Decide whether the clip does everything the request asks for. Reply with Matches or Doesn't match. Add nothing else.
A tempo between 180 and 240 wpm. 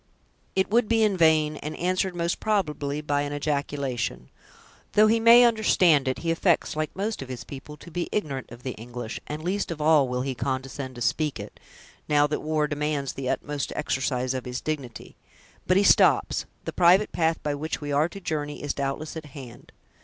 Matches